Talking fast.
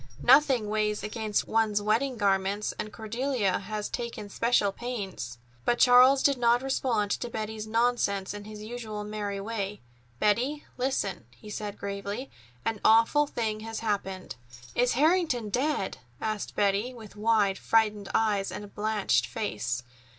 No: average, 140 wpm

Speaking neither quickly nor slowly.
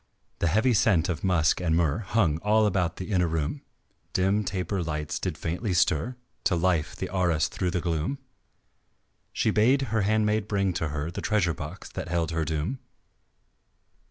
Yes: average, 170 wpm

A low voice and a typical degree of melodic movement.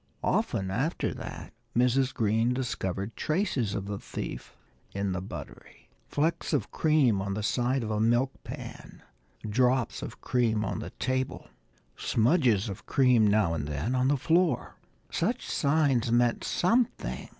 Yes: low, 120 Hz; average, 4.3 semitones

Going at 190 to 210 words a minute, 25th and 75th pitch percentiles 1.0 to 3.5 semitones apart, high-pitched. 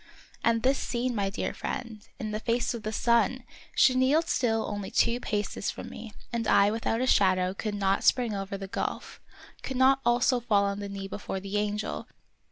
Yes: average, 195 wpm; average, 3.2 semitones; high, 220 Hz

